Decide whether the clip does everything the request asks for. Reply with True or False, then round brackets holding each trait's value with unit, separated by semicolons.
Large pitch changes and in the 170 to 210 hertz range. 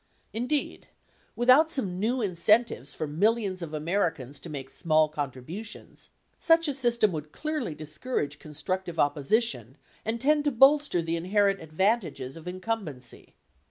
True (7.4 semitones; 185 Hz)